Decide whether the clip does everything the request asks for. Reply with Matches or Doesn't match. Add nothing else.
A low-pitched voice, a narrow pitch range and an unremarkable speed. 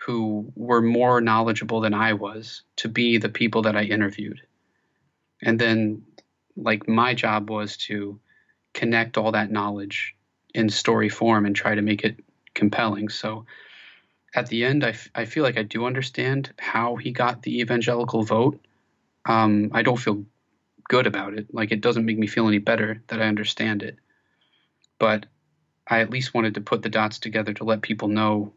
Matches